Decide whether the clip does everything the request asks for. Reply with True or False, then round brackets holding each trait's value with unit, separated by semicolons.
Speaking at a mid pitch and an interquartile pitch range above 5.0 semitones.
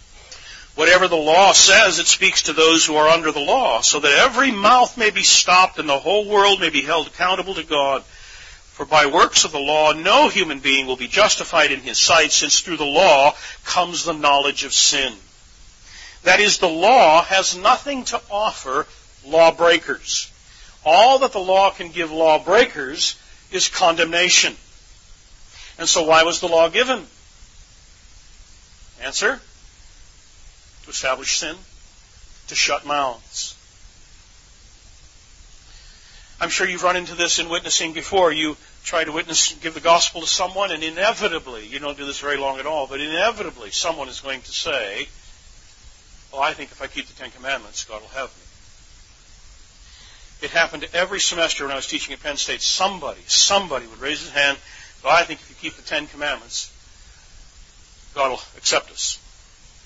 True (155 Hz; 5.6 semitones)